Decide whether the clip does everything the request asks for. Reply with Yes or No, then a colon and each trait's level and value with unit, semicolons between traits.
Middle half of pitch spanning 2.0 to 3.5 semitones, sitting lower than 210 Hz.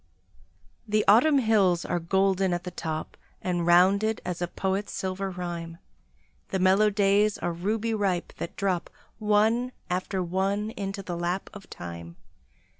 Yes: average, 2.9 semitones; high, 190 Hz